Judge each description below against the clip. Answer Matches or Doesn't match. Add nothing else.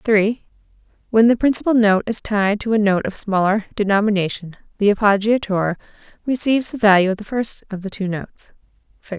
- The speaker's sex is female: Matches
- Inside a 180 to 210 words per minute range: Doesn't match